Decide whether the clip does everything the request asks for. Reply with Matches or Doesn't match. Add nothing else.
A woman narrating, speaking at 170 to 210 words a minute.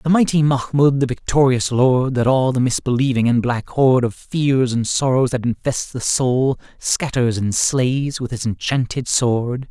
Doesn't match